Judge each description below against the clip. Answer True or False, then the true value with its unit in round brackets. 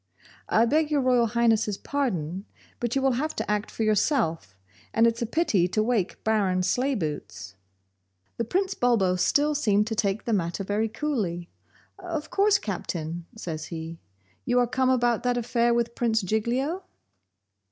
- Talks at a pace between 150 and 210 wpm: True (160 wpm)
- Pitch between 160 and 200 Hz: False (225 Hz)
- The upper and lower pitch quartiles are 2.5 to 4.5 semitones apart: False (5.0 semitones)